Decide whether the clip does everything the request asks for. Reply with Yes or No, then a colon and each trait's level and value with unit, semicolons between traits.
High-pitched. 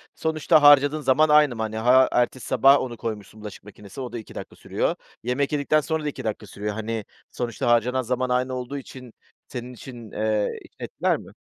No: low, 125 Hz